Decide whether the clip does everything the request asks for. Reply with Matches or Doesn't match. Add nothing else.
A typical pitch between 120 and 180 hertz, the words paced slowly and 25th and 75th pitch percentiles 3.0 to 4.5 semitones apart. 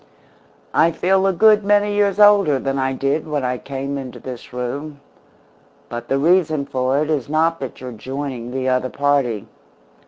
Doesn't match